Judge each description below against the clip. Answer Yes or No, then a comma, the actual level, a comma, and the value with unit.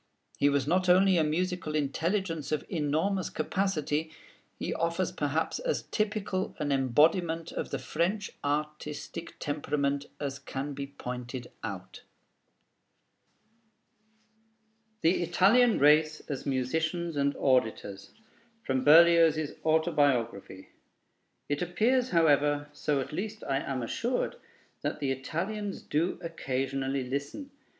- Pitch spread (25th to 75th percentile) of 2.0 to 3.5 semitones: No, average, 3.9 semitones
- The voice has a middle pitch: Yes, medium, 150 Hz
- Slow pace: Yes, slow, 110 wpm